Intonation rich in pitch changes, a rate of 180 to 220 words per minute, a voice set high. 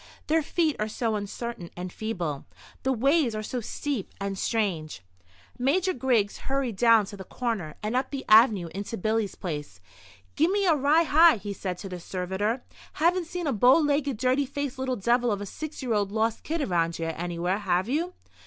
Yes: wide, 6.2 semitones; average, 190 wpm; high, 225 Hz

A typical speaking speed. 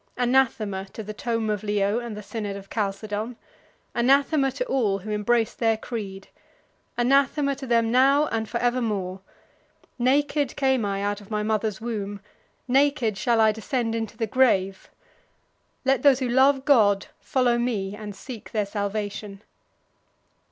Yes: average, 145 wpm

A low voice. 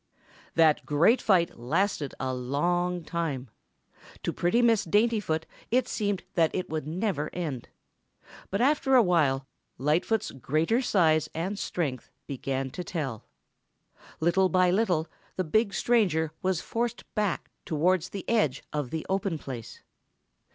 No: medium, 175 Hz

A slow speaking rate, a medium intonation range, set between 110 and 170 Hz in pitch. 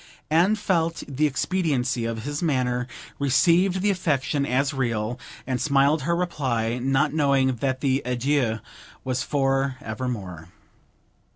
Yes: slow, 125 wpm; average, 3.6 semitones; low, 135 Hz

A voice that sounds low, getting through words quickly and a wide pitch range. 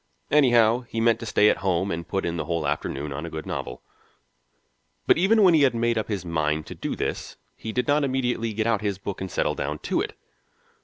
Yes: low, 105 Hz; fast, 230 wpm; wide, 6.1 semitones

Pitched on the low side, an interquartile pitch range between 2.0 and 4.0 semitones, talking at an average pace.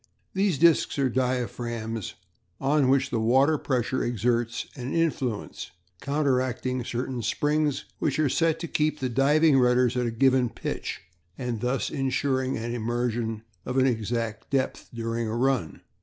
Yes: low, 125 Hz; average, 2.7 semitones; average, 145 wpm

